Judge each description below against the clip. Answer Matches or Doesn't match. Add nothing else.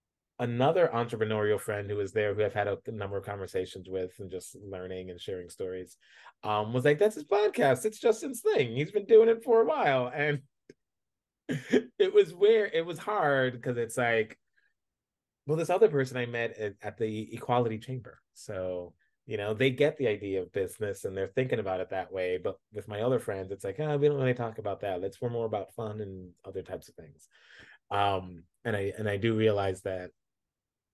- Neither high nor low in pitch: Doesn't match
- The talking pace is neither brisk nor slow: Doesn't match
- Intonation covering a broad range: Matches